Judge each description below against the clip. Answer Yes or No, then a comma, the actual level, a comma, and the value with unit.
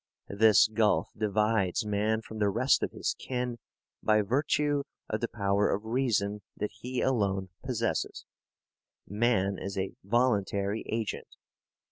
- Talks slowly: Yes, slow, 130 wpm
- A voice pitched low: Yes, low, 110 Hz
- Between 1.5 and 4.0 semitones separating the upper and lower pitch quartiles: Yes, average, 2.9 semitones